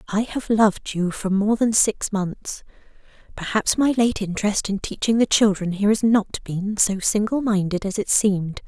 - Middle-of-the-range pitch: No, high, 205 Hz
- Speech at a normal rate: Yes, average, 185 wpm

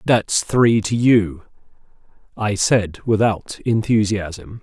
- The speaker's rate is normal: No, slow, 105 wpm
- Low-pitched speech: Yes, low, 105 Hz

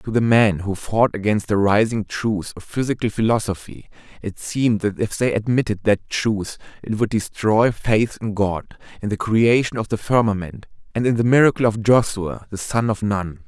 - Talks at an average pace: Yes, average, 185 wpm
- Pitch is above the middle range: No, low, 110 Hz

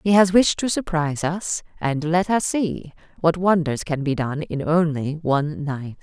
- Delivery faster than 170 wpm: Yes, average, 190 wpm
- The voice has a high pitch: No, medium, 165 Hz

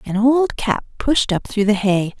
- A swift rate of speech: Yes, fast, 220 wpm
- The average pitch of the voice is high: Yes, high, 220 Hz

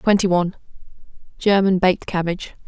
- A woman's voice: Yes, female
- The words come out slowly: Yes, slow, 90 wpm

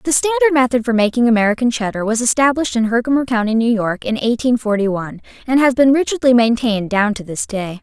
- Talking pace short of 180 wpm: No, fast, 205 wpm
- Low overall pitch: No, high, 235 Hz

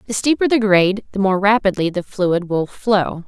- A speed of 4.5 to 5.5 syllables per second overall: Yes, 5.0 syllables/s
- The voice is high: Yes, high, 200 Hz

